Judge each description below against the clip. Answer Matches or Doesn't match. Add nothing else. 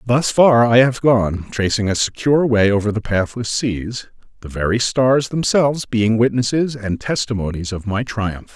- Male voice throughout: Matches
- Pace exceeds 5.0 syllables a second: Doesn't match